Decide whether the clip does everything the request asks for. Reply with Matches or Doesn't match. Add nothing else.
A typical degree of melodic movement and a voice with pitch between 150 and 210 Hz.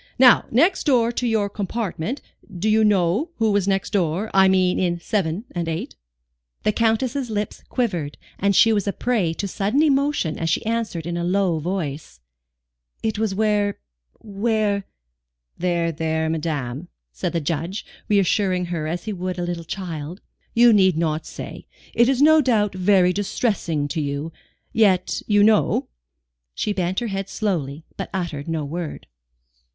Matches